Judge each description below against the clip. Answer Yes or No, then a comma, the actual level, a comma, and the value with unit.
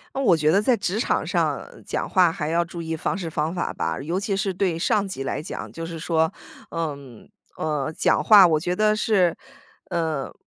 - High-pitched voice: No, medium, 170 Hz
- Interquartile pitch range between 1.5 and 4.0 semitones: Yes, average, 3.4 semitones